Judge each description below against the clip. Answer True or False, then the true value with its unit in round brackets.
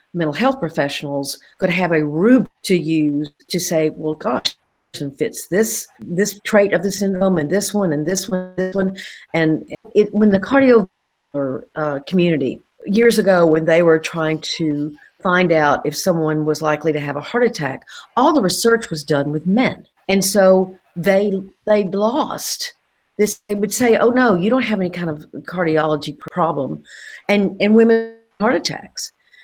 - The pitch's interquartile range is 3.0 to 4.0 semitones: False (4.9 semitones)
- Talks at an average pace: True (170 wpm)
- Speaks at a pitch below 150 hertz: False (185 Hz)